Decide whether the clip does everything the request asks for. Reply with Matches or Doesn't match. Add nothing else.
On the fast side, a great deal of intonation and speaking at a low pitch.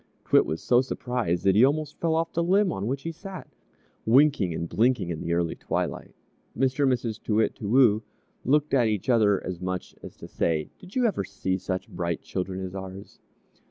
Matches